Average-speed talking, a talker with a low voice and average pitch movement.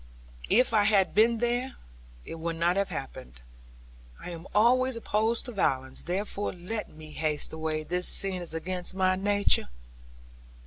No: average, 150 wpm; medium, 185 Hz; average, 4.8 semitones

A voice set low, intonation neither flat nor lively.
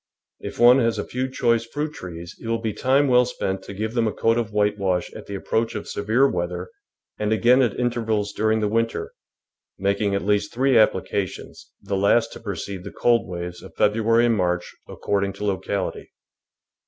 Yes: low, 110 Hz; average, 3.0 semitones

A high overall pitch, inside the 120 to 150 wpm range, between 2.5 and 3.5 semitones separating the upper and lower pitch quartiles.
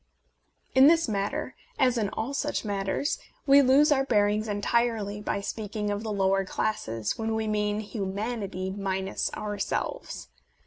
Yes: high, 210 Hz; average, 145 wpm; average, 3.0 semitones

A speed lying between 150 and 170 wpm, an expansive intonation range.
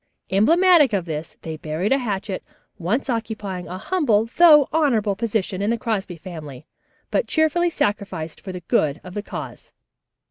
Yes: average, 155 wpm; wide, 6.5 semitones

